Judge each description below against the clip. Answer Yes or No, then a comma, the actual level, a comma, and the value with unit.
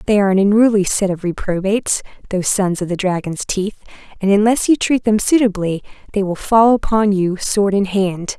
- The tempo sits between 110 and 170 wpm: No, average, 195 wpm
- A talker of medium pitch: No, high, 200 Hz